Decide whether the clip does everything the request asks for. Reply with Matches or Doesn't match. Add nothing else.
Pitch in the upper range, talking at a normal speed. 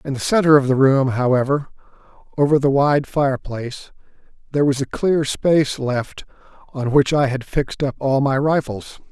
Doesn't match